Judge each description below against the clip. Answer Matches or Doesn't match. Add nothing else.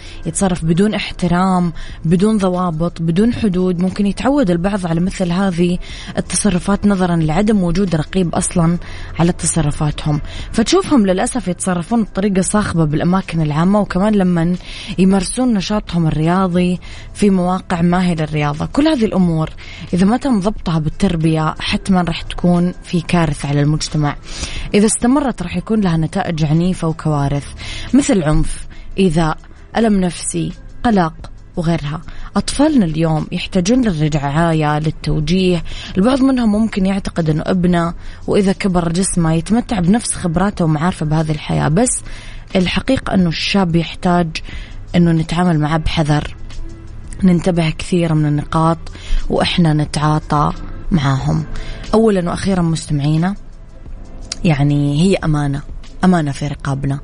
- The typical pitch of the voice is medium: Matches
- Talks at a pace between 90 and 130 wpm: Matches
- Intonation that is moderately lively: Matches